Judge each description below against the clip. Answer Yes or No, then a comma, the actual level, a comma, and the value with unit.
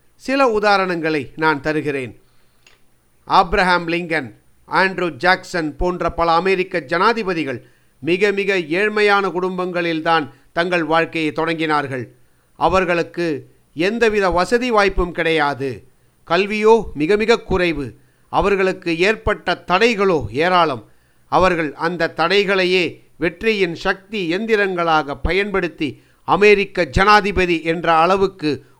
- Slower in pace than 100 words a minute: Yes, average, 90 wpm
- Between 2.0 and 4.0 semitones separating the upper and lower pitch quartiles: Yes, average, 3.4 semitones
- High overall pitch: No, medium, 175 Hz